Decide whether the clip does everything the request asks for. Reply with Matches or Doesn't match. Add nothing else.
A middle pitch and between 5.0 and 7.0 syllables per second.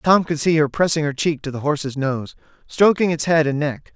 Matches